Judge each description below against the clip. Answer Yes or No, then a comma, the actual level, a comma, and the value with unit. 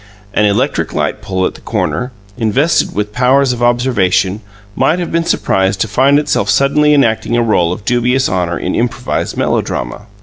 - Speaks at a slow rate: No, average, 170 wpm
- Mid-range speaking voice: No, low, 120 Hz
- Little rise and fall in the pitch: No, average, 4.9 semitones